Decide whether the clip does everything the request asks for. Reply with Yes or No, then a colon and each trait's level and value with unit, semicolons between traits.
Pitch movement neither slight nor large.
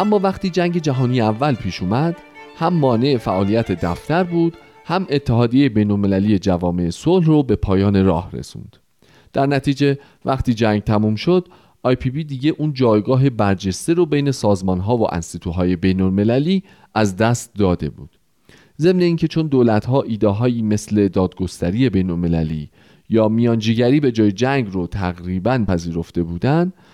No: wide, 6.9 semitones